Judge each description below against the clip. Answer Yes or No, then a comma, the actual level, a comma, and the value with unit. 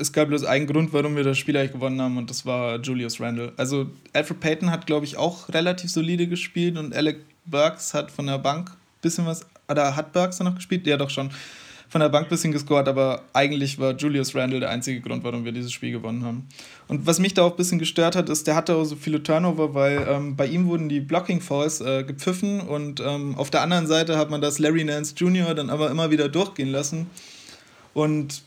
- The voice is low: No, medium, 150 Hz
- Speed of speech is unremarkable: No, fast, 235 wpm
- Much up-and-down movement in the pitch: No, average, 3.1 semitones